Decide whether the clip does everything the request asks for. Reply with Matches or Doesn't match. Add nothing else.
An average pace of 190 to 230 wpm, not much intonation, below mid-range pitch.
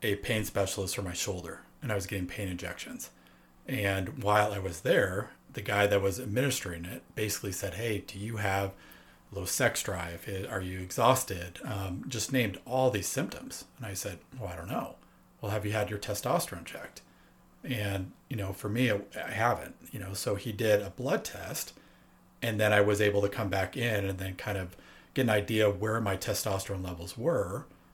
Matches